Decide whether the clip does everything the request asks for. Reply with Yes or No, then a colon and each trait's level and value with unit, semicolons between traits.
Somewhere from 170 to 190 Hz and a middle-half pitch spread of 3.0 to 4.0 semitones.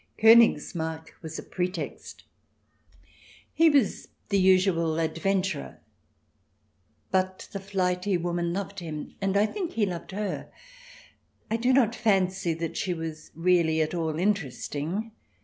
Yes: medium, 185 Hz; average, 3.4 semitones